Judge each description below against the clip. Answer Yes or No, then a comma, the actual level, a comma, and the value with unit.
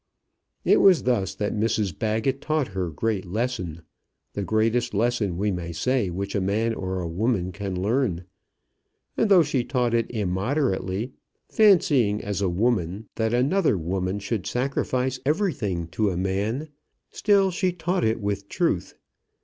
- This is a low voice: Yes, low, 110 Hz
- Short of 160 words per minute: Yes, average, 150 wpm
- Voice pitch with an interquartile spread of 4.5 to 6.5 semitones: Yes, average, 5.1 semitones